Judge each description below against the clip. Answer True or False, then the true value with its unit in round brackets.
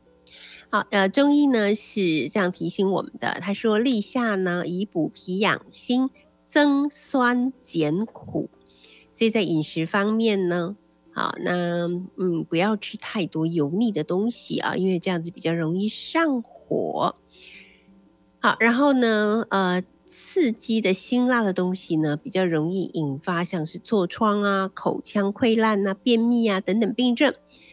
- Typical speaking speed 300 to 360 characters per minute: False (210 characters per minute)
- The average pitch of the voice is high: True (195 Hz)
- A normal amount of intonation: True (4.6 semitones)